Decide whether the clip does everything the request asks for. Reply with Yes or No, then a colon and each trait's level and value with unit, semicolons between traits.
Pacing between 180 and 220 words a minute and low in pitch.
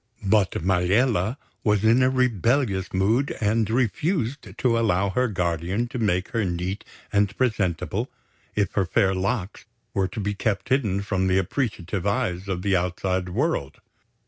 No: average, 150 wpm; low, 100 Hz